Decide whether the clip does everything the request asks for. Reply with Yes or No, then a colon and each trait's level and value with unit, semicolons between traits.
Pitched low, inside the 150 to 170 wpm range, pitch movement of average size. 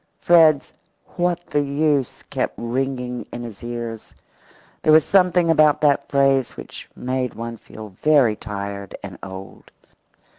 No: low, 130 Hz; slow, 135 wpm; average, 5.0 semitones